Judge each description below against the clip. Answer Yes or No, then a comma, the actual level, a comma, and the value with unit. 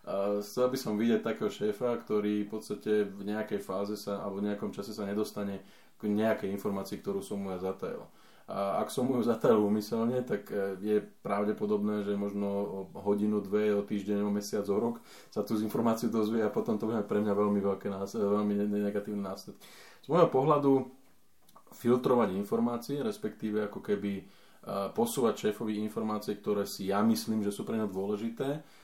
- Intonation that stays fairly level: Yes, narrow, 1.7 semitones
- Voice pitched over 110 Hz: No, low, 105 Hz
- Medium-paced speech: No, fast, 175 wpm